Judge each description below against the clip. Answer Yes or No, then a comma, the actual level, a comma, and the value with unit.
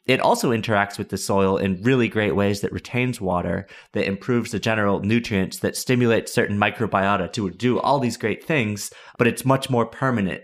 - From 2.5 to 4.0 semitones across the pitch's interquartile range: Yes, average, 3.4 semitones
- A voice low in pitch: Yes, low, 105 Hz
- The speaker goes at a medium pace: Yes, average, 190 wpm